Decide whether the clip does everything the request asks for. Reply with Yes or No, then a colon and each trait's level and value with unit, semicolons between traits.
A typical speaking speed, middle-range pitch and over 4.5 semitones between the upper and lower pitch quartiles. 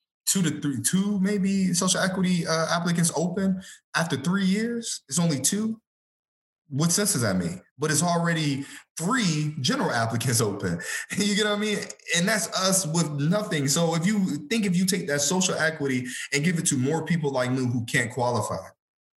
Yes: average, 185 wpm; medium, 170 Hz; wide, 5.4 semitones